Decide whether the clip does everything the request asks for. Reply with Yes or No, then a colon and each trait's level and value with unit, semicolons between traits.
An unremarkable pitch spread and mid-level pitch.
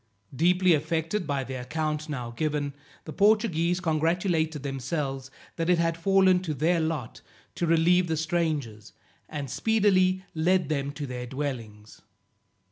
Yes: average, 4.0 semitones; medium, 160 Hz